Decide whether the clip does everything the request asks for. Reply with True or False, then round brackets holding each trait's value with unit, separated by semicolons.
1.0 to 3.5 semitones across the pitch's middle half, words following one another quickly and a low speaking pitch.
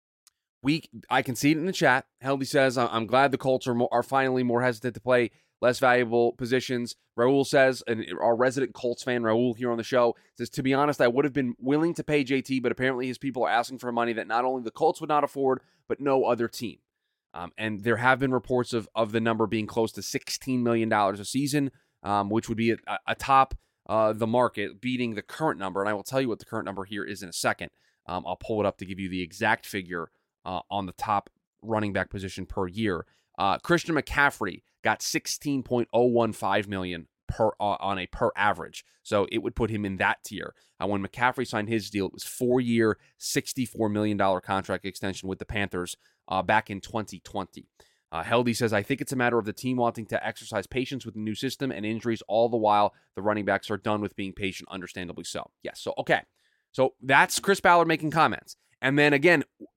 False (4.2 semitones; 220 wpm; 115 Hz)